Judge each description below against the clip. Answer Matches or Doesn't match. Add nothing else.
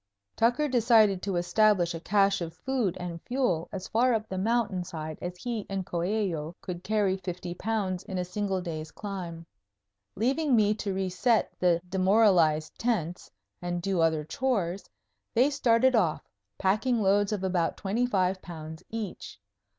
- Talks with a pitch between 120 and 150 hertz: Doesn't match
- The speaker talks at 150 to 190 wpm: Matches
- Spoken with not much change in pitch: Doesn't match